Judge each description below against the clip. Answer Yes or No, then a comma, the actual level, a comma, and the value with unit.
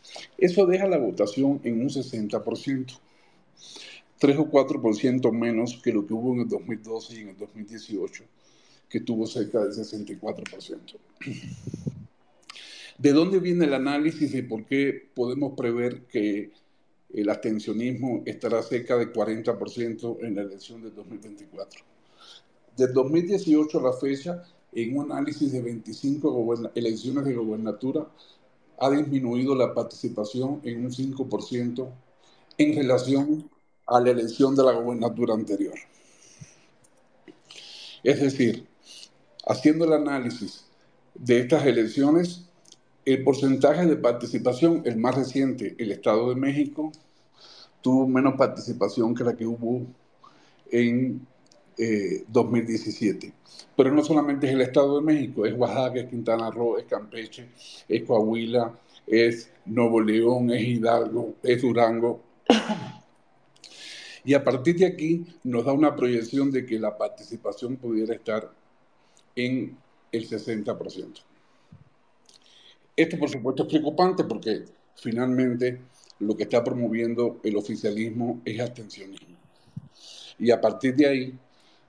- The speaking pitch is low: Yes, low, 125 Hz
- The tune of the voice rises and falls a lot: No, average, 3.3 semitones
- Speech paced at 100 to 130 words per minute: Yes, slow, 125 wpm